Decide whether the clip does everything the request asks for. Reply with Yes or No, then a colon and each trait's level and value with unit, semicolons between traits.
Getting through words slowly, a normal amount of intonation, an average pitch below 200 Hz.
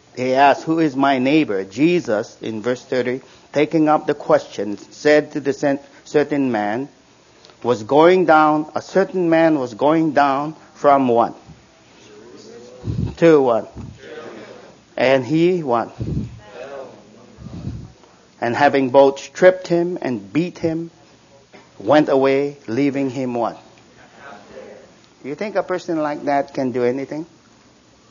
Yes: slow, 120 wpm; average, 3.6 semitones; medium, 140 Hz